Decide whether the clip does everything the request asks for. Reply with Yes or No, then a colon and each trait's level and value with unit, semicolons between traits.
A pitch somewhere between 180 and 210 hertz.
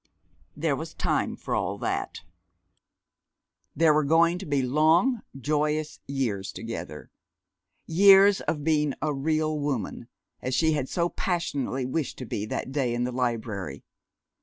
No: medium, 150 Hz